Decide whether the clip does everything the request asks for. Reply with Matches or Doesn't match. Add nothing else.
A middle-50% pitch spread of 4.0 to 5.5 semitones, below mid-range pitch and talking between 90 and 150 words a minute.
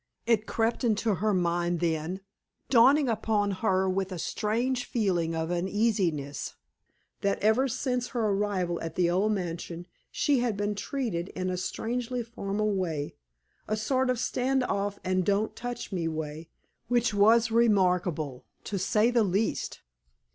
Doesn't match